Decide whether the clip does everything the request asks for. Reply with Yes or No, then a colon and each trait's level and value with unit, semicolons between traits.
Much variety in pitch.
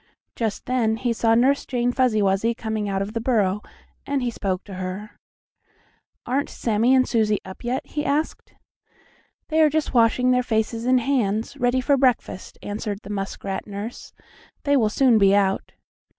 No: average, 3.6 semitones